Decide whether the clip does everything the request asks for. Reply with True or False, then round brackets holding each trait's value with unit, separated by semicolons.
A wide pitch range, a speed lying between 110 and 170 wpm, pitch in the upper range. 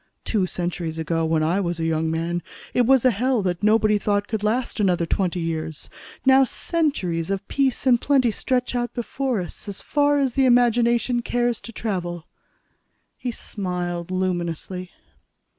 True (5.9 semitones; 160 wpm; 205 Hz)